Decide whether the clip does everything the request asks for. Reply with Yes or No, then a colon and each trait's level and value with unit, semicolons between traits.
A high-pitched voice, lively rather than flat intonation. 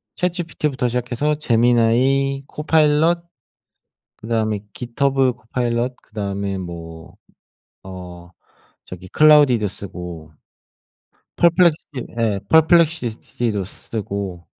No: low, 120 Hz; wide, 6.9 semitones